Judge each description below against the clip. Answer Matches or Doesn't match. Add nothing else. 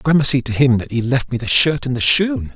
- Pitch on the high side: Doesn't match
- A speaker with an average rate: Doesn't match